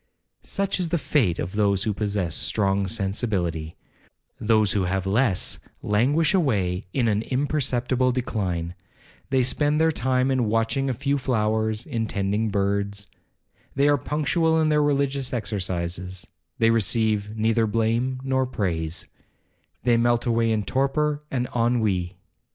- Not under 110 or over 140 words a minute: Yes, slow, 135 wpm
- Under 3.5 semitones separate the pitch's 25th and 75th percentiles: No, average, 4.7 semitones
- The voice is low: Yes, low, 115 Hz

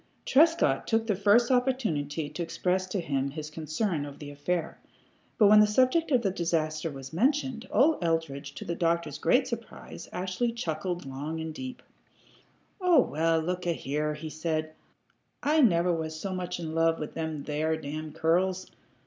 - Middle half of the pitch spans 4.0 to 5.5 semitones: Yes, average, 5.1 semitones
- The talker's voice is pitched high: No, medium, 165 Hz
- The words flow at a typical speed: Yes, average, 170 wpm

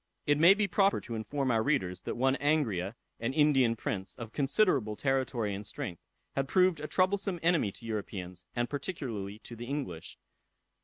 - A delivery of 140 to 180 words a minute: Yes, average, 170 wpm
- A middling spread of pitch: No, wide, 5.9 semitones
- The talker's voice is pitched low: Yes, low, 130 Hz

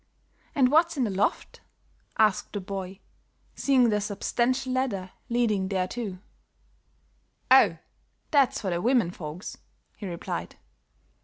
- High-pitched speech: Yes, high, 210 Hz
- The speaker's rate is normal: No, slow, 120 wpm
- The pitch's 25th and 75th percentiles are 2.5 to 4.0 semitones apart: No, average, 5.1 semitones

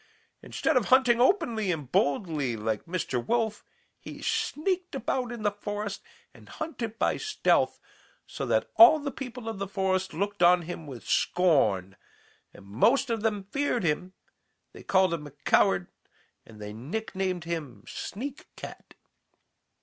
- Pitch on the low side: No, high, 195 Hz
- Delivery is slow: No, average, 150 wpm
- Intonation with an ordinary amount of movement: No, wide, 7.9 semitones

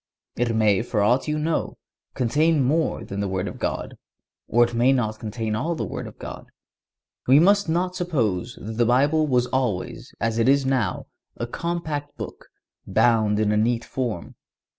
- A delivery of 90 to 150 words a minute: No, average, 180 wpm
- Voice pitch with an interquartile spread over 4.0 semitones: Yes, average, 5.3 semitones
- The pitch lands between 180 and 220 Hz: No, low, 120 Hz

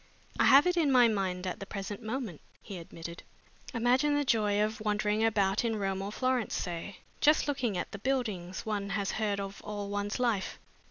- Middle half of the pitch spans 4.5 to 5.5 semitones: No, average, 3.7 semitones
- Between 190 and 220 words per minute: Yes, average, 195 wpm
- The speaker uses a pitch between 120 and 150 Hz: No, high, 210 Hz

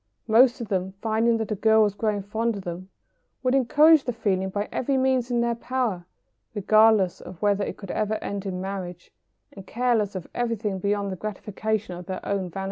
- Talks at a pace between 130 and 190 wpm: No, average, 200 wpm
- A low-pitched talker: No, high, 210 Hz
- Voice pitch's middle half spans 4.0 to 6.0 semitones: No, average, 3.4 semitones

